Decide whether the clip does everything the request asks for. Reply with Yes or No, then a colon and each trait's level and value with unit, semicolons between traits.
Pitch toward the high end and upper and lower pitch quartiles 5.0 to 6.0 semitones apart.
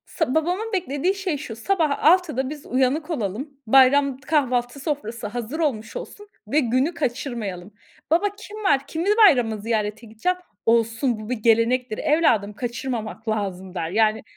Yes: very high, 255 Hz; wide, 5.6 semitones